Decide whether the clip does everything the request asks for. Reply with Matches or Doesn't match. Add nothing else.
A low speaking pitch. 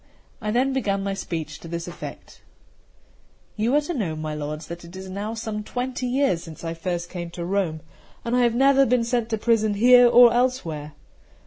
Doesn't match